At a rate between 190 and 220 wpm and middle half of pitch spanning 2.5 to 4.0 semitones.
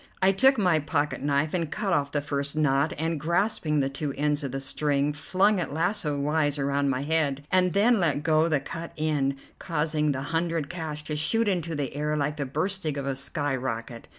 Yes: fast, 205 wpm; average, 2.9 semitones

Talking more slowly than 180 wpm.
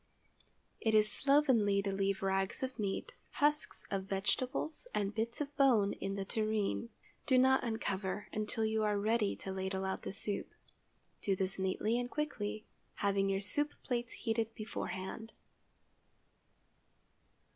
Yes: average, 140 wpm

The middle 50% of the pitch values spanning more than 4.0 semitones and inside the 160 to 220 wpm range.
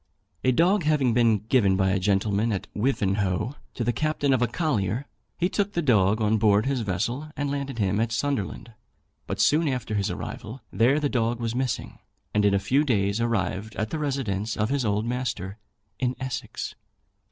Yes: average, 4.6 semitones; average, 190 wpm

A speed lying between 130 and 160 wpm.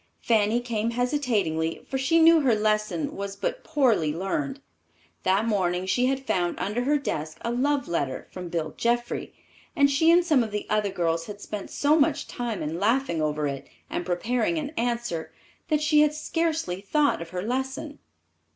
No: average, 180 wpm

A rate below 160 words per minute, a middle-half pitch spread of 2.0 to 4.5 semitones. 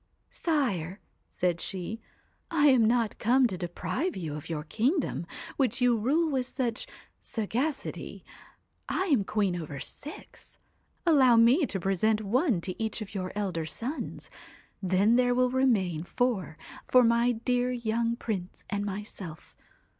No: average, 150 wpm; average, 5.1 semitones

